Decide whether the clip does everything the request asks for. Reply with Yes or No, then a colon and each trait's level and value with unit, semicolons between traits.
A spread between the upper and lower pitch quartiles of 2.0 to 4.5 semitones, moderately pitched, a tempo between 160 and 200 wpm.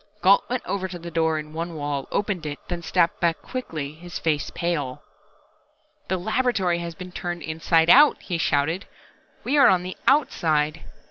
Yes: average, 2.9 semitones; medium, 170 Hz; average, 180 wpm